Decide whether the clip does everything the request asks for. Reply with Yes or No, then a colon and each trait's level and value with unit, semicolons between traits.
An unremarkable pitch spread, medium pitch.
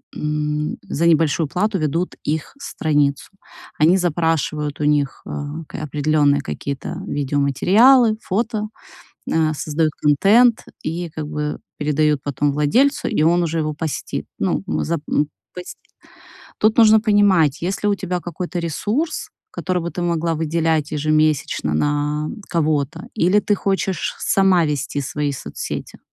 Yes: average, 3.6 semitones; medium, 160 Hz